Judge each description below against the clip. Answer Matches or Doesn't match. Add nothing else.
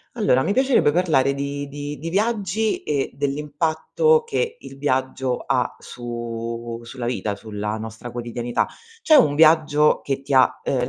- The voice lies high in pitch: Doesn't match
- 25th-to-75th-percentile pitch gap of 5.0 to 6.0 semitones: Matches